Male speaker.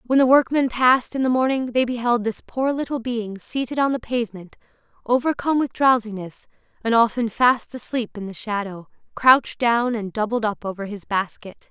No: female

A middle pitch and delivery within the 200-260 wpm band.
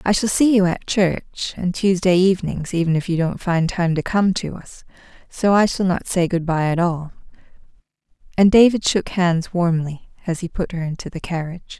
Yes: medium, 180 Hz; fast, 205 wpm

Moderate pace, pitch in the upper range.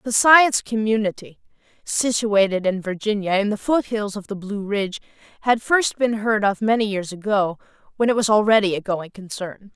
Yes: average, 170 wpm; high, 210 Hz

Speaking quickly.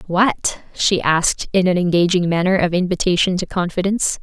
No: average, 155 wpm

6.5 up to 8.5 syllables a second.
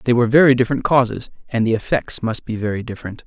Yes: 7.1 syllables/s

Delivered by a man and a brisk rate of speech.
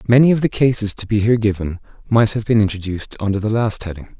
Yes: male; fast, 230 wpm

